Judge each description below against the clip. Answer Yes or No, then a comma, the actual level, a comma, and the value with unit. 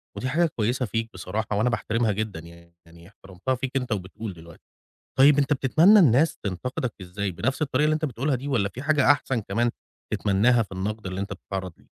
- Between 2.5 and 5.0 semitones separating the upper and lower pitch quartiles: No, wide, 5.4 semitones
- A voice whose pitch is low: Yes, low, 115 Hz